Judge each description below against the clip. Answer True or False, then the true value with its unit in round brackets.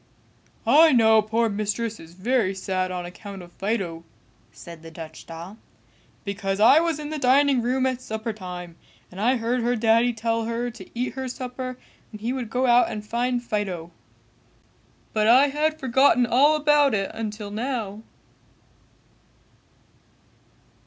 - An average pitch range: True (4.1 semitones)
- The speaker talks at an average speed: True (150 wpm)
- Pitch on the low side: False (230 Hz)